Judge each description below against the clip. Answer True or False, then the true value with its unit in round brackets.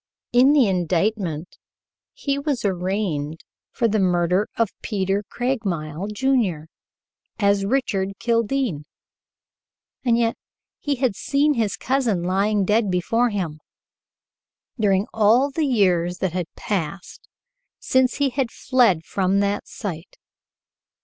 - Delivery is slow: True (115 wpm)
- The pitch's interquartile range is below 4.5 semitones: False (5.0 semitones)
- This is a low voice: False (205 Hz)